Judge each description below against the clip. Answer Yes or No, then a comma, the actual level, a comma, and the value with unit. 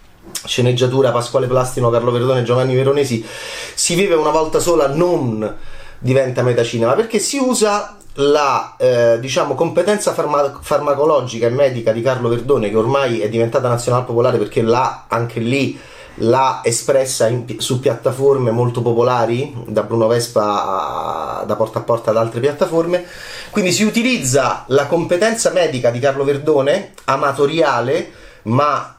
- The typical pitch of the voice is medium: No, low, 130 Hz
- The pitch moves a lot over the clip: No, average, 4.0 semitones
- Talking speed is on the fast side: No, average, 140 wpm